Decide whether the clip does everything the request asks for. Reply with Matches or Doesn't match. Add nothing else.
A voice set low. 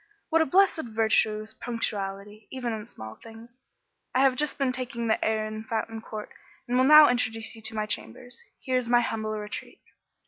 Doesn't match